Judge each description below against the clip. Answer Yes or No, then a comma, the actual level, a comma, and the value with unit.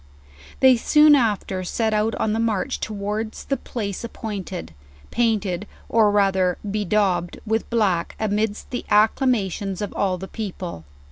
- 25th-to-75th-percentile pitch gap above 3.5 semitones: No, average, 2.7 semitones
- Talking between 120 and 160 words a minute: Yes, average, 140 wpm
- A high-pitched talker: Yes, high, 210 Hz